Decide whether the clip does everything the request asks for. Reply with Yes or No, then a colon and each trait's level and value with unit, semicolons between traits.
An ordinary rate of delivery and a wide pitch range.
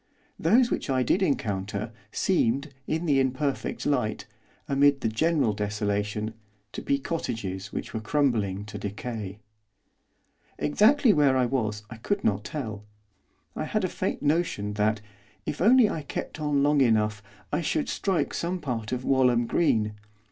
Yes: average, 150 wpm; wide, 5.9 semitones